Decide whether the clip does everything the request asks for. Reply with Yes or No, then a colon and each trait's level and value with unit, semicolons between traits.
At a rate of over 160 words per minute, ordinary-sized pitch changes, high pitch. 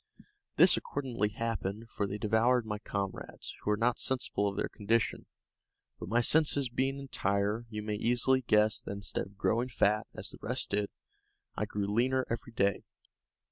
No: average, 170 wpm; average, 3.0 semitones; low, 110 Hz